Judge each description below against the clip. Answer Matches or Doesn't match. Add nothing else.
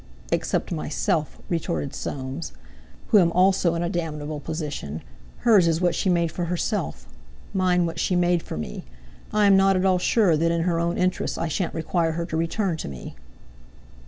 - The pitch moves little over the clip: Matches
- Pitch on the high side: Doesn't match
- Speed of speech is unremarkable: Matches